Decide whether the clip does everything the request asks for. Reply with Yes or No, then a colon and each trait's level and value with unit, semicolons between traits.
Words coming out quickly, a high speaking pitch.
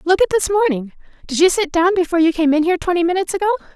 Yes: fast, 240 wpm; very high, 350 Hz